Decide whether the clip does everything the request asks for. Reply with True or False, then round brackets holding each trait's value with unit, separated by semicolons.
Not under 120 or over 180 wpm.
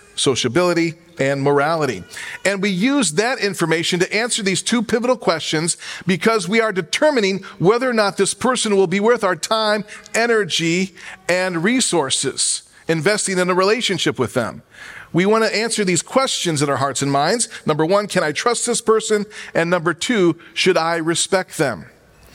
True (165 wpm)